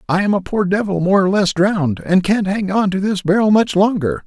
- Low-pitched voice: No, high, 195 Hz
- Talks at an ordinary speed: No, fast, 255 wpm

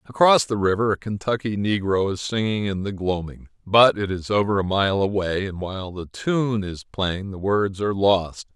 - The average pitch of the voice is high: No, low, 100 Hz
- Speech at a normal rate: Yes, average, 195 wpm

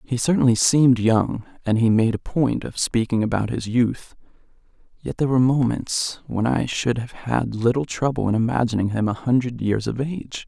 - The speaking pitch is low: Yes, low, 120 Hz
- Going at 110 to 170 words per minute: No, average, 180 wpm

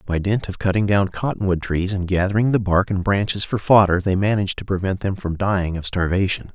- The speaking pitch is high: No, very low, 95 Hz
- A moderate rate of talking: No, fast, 220 wpm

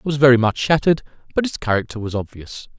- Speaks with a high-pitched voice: No, low, 130 Hz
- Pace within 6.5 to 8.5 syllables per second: Yes, 6.8 syllables/s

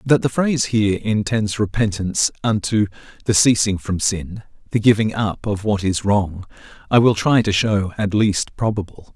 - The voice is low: Yes, low, 105 Hz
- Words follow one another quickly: No, average, 170 wpm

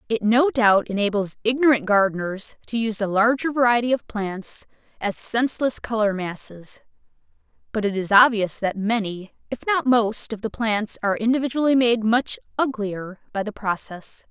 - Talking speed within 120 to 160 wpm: Yes, average, 155 wpm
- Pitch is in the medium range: No, high, 220 Hz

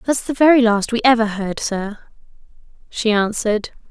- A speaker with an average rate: Yes, average, 155 wpm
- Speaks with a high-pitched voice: Yes, high, 225 Hz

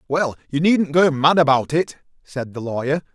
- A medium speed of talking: Yes, average, 190 wpm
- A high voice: No, medium, 150 Hz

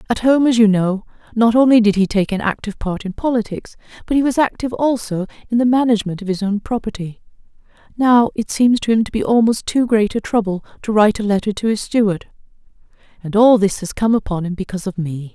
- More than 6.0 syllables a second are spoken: Yes, 6.2 syllables/s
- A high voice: Yes, high, 215 Hz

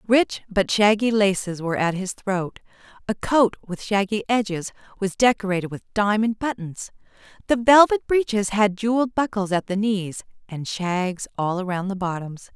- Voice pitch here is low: No, high, 205 Hz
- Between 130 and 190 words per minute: Yes, average, 160 wpm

